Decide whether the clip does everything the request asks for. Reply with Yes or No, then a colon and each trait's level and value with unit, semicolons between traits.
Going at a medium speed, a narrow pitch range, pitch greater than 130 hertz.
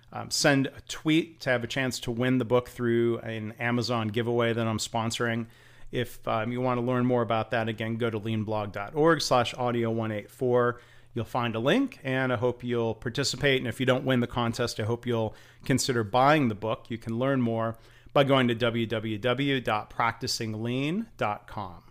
No: average, 180 wpm; narrow, 1.9 semitones; low, 120 Hz